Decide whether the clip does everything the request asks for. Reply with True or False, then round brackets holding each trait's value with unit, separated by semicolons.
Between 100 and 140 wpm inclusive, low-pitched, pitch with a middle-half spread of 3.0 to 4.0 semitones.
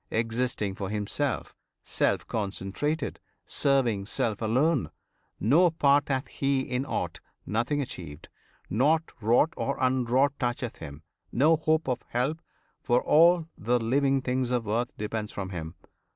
False (135 wpm; 125 Hz; 4.6 semitones)